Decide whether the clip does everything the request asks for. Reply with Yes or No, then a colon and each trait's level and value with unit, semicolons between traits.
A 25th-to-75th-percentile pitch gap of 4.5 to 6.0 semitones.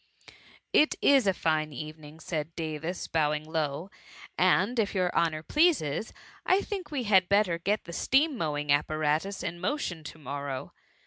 Yes: average, 5.0 semitones